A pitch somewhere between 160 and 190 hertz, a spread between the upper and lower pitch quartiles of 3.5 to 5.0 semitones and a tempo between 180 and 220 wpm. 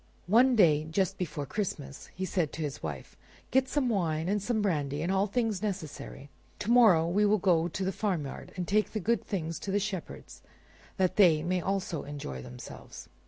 Yes: medium, 185 Hz; average, 4.7 semitones; average, 190 wpm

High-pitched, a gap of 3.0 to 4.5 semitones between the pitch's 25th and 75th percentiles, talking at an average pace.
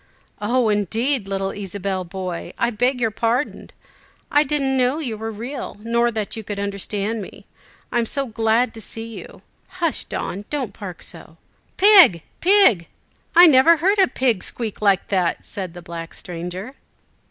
No: high, 225 Hz; average, 4.9 semitones; average, 165 wpm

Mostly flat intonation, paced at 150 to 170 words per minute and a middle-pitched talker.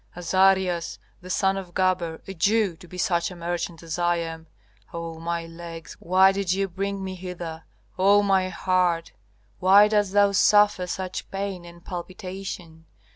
Yes: narrow, 2.1 semitones; average, 160 wpm; medium, 180 Hz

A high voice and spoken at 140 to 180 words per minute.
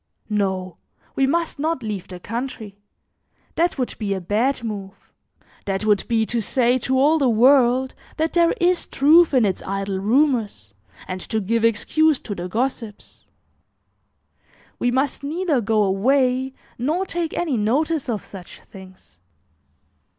Yes: high, 240 Hz; average, 145 wpm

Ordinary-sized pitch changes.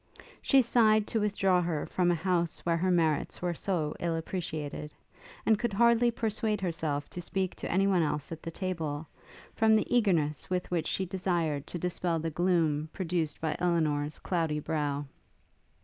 Yes: average, 3.5 semitones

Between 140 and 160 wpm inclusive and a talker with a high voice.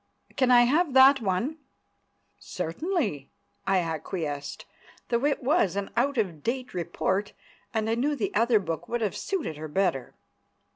Yes: average, 150 wpm; high, 220 Hz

